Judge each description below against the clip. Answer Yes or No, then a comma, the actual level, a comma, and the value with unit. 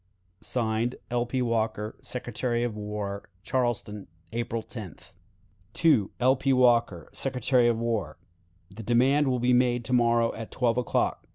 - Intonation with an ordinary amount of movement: No, narrow, 2.2 semitones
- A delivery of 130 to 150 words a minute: Yes, average, 140 wpm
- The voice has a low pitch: Yes, low, 120 Hz